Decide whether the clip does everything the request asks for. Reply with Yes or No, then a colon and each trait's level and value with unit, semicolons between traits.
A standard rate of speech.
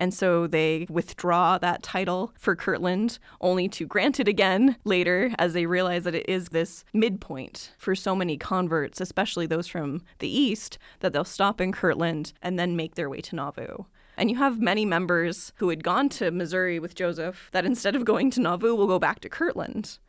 Yes: average, 195 wpm